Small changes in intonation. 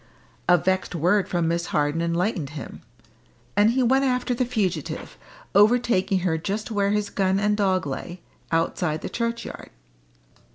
No: average, 4.3 semitones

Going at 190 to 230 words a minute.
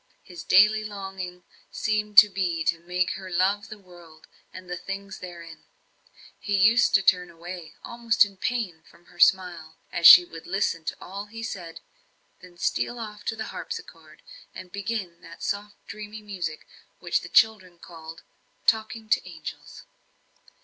No: average, 155 wpm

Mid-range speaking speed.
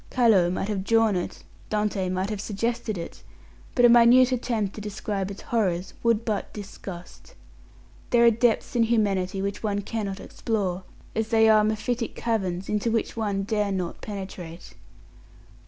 Yes: average, 155 wpm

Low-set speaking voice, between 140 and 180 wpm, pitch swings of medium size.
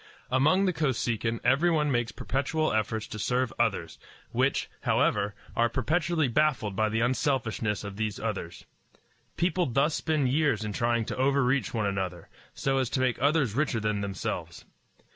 Yes: low, 125 Hz; average, 155 wpm; average, 4.8 semitones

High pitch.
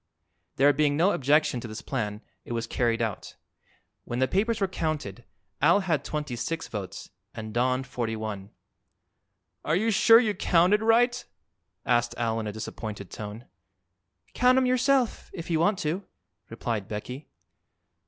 No: low, 135 Hz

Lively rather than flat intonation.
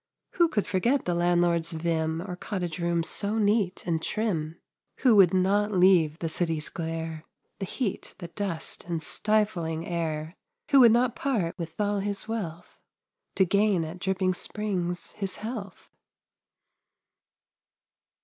No: average, 3.7 semitones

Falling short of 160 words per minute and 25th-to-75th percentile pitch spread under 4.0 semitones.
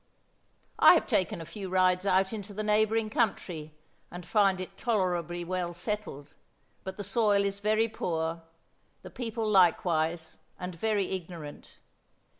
Yes: average, 140 wpm; average, 3.5 semitones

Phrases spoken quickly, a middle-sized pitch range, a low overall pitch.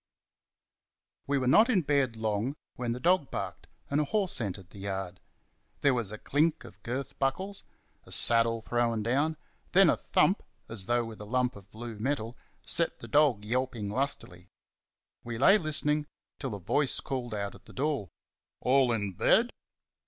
No: average, 170 wpm; average, 4.9 semitones; low, 125 Hz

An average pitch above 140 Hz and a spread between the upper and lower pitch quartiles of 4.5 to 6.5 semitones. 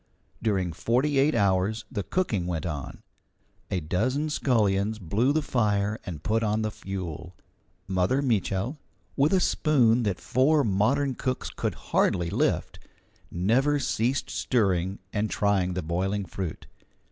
No: low, 105 Hz; wide, 5.6 semitones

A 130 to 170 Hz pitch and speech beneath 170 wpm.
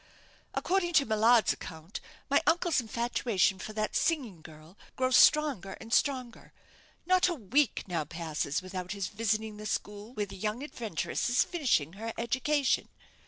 No: high, 220 Hz; average, 150 wpm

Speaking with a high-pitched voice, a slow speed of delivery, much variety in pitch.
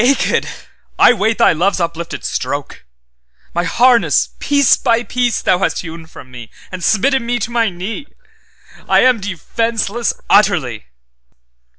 Yes: high, 200 Hz; slow, 120 wpm; wide, 6.4 semitones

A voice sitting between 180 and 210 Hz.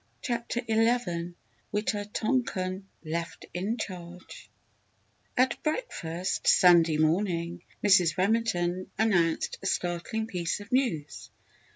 Yes: medium, 185 Hz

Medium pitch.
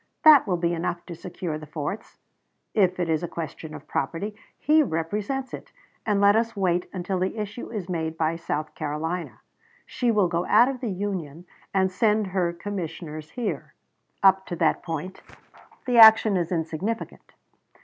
Yes: medium, 180 Hz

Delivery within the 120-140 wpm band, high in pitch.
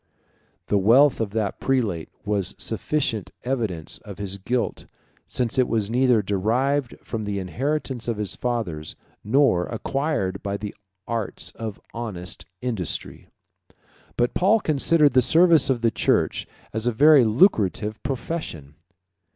No: slow, 135 wpm; low, 115 Hz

